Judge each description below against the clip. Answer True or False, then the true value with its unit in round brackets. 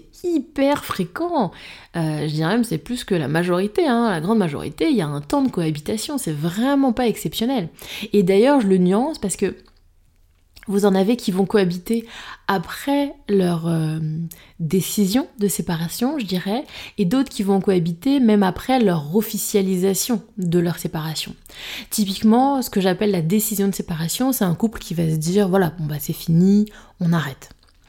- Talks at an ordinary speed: True (175 wpm)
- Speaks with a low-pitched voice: False (195 Hz)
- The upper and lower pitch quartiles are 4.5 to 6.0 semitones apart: True (5.1 semitones)